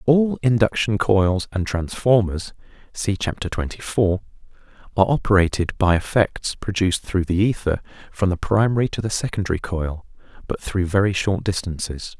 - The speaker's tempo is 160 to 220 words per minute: No, average, 140 wpm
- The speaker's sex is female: No, male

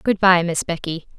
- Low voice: No, medium, 175 Hz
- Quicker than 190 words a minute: Yes, fast, 205 wpm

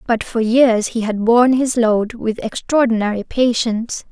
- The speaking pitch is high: Yes, high, 230 Hz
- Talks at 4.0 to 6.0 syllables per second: Yes, 4.6 syllables/s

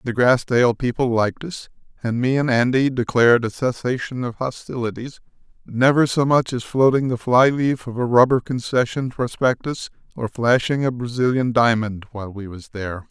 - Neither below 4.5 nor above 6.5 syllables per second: Yes, 5.2 syllables/s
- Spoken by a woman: No, male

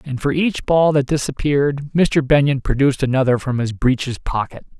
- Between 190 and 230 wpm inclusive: No, average, 175 wpm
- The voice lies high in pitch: No, medium, 140 Hz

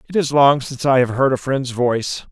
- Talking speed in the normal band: No, fast, 260 wpm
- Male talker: Yes, male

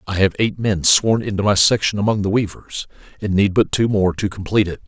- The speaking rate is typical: No, fast, 235 wpm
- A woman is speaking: No, male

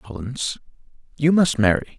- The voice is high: No, low, 130 Hz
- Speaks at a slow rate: Yes, slow, 120 wpm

